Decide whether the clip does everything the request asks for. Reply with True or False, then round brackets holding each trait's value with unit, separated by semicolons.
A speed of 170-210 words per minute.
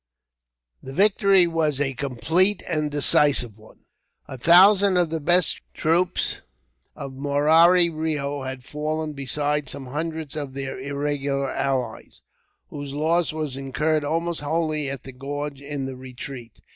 False (135 wpm)